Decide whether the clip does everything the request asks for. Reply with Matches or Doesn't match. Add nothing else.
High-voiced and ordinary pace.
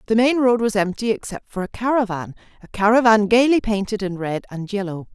Matches